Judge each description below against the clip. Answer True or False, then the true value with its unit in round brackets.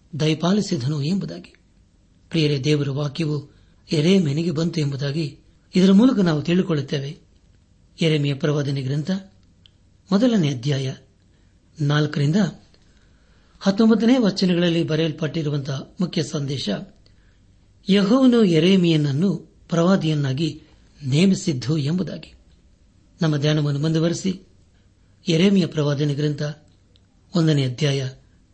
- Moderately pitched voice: True (150 Hz)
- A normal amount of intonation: False (8.5 semitones)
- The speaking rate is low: False (75 wpm)